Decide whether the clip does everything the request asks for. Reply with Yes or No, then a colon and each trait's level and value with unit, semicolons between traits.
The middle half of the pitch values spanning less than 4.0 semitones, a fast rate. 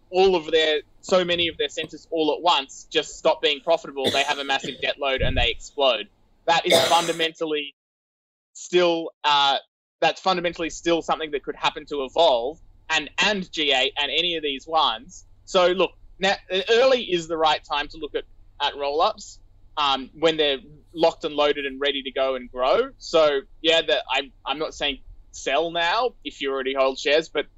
No: average, 3.5 semitones; average, 185 wpm